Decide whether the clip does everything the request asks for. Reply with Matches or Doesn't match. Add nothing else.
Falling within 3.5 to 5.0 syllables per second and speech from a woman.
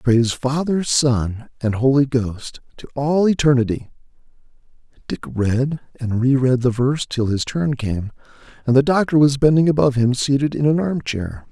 Doesn't match